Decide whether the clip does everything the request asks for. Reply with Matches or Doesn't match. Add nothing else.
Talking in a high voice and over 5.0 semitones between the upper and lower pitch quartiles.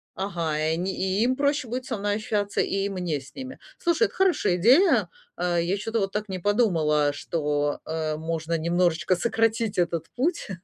Matches